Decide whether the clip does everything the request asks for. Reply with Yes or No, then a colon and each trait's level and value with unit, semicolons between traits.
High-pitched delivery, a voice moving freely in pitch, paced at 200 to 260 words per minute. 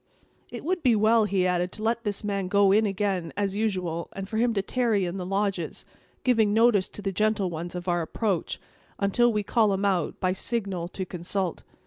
No: high, 200 Hz; average, 2.9 semitones; fast, 205 wpm